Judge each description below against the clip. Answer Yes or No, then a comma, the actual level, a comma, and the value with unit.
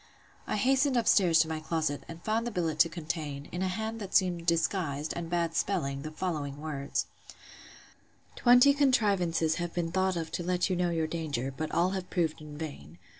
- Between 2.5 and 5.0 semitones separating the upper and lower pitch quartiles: Yes, average, 3.2 semitones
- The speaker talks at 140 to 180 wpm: No, average, 195 wpm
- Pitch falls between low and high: Yes, medium, 170 Hz